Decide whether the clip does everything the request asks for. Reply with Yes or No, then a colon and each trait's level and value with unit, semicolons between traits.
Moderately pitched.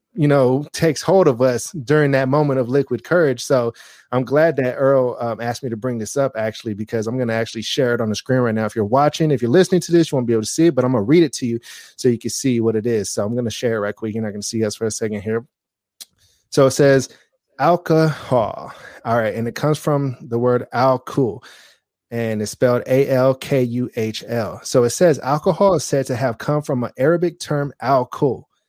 No: low, 130 Hz